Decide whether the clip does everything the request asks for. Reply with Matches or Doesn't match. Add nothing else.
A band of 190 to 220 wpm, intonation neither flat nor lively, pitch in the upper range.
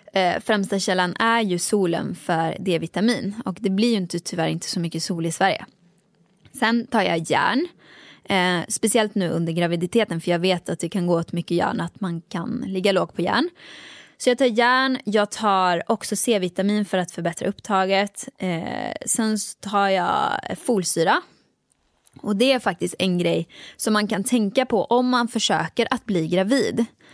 Doesn't match